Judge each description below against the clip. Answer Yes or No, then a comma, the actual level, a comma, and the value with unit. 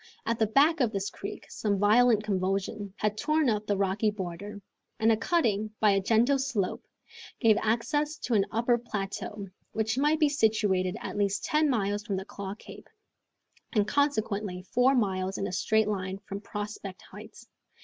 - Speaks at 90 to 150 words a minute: No, average, 170 wpm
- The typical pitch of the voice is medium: No, high, 215 Hz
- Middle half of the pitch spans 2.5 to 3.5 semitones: Yes, average, 3.1 semitones